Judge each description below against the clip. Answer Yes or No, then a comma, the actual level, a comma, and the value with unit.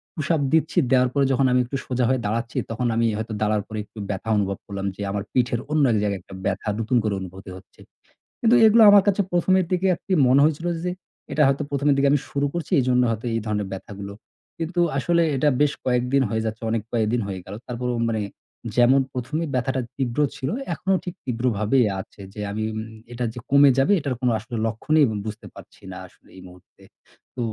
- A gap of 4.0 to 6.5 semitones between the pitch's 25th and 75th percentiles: Yes, average, 4.6 semitones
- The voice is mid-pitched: No, low, 125 Hz